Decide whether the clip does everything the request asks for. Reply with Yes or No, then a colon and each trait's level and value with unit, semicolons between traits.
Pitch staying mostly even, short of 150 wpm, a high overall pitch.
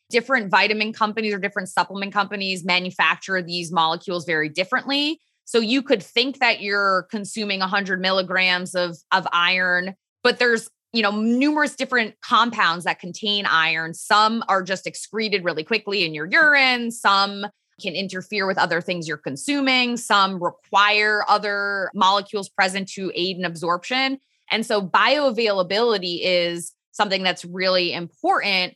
No: average, 3.7 semitones; average, 140 wpm; high, 200 Hz